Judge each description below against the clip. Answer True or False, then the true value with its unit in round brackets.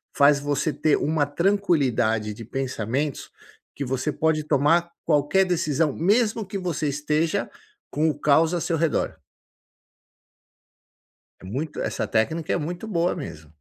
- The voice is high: False (150 Hz)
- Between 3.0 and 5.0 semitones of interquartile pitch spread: True (3.3 semitones)